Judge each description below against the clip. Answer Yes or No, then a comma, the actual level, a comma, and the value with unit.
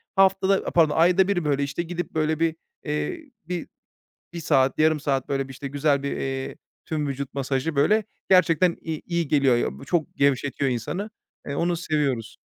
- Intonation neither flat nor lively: Yes, average, 3.9 semitones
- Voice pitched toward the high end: No, medium, 155 Hz